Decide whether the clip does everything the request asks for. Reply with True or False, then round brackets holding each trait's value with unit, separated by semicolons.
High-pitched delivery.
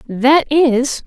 True (270 Hz)